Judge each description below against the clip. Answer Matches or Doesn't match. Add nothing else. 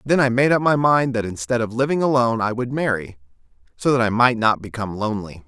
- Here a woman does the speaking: Doesn't match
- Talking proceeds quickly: Matches